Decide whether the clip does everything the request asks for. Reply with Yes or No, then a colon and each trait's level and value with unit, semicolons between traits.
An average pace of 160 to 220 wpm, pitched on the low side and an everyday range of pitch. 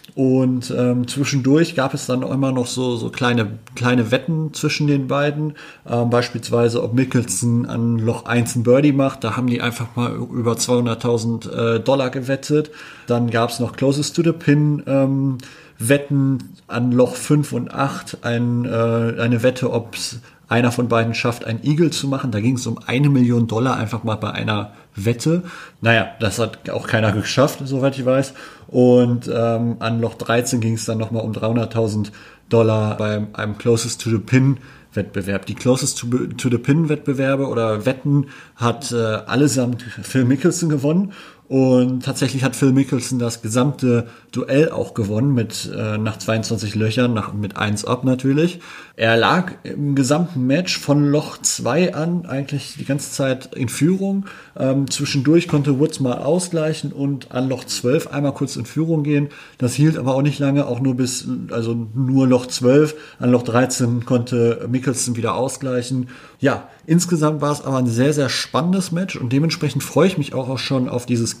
Yes: average, 175 wpm; low, 125 Hz; average, 3.2 semitones